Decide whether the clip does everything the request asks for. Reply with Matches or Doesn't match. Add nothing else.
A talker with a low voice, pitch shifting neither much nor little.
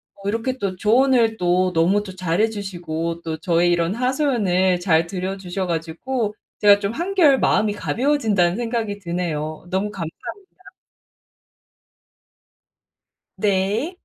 Doesn't match